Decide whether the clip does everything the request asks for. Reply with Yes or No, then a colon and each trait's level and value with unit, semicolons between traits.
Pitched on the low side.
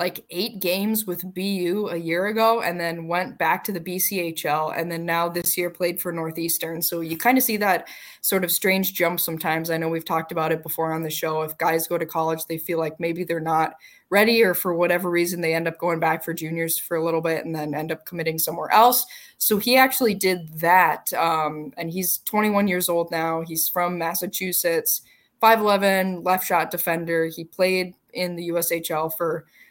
No: medium, 170 Hz